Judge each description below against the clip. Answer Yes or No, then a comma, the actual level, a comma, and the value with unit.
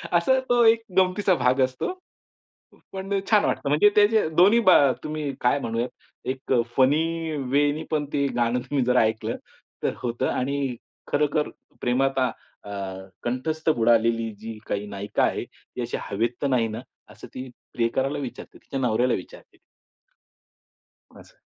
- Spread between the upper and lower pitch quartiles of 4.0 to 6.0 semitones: Yes, average, 4.8 semitones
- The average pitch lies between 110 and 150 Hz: Yes, low, 135 Hz